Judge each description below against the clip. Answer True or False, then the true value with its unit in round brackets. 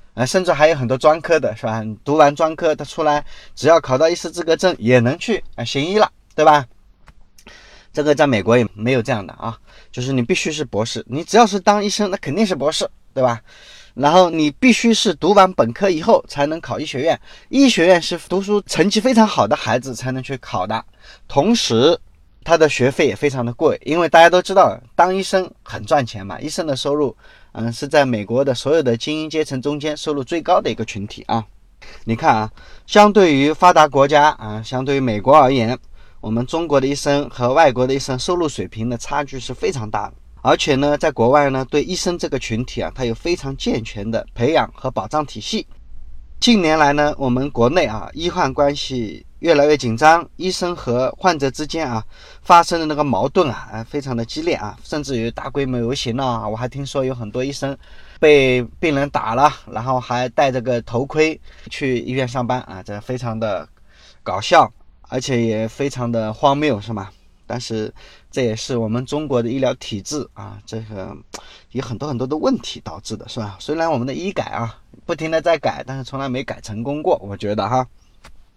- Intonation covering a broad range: False (5.0 semitones)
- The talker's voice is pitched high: False (135 Hz)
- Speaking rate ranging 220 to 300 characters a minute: True (295 characters per minute)